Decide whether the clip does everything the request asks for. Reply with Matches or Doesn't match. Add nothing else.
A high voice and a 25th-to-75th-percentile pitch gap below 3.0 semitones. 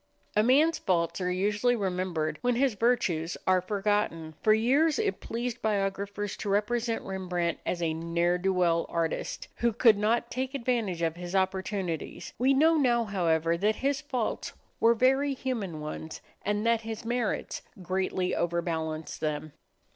Doesn't match